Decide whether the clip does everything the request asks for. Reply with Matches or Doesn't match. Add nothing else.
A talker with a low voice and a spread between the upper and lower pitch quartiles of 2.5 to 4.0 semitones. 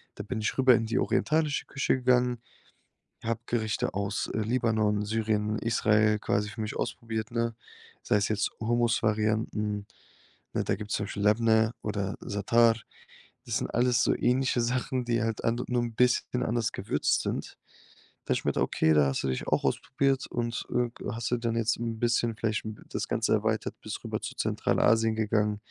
Doesn't match